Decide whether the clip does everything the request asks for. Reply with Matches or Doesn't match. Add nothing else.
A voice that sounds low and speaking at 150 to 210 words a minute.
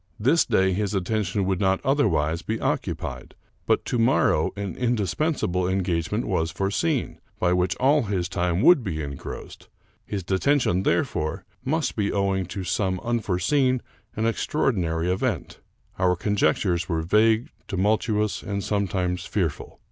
Doesn't match